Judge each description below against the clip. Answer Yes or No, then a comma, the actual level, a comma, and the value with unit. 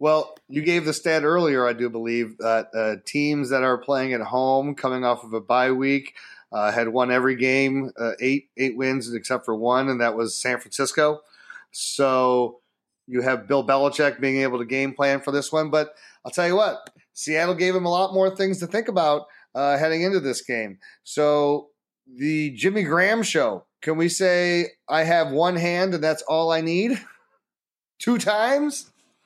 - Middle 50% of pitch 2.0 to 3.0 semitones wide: No, average, 5.0 semitones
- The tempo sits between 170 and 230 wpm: Yes, average, 190 wpm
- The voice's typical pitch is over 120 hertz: Yes, medium, 140 Hz